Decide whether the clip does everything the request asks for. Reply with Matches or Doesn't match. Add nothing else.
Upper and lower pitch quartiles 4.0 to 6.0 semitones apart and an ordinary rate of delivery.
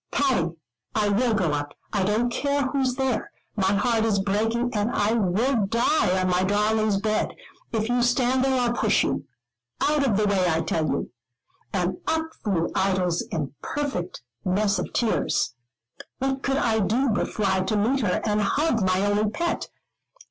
Matches